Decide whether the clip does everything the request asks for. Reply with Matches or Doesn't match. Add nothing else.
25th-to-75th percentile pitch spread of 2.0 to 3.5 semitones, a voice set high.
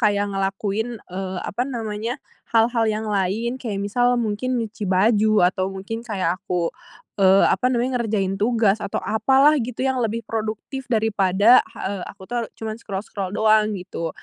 Matches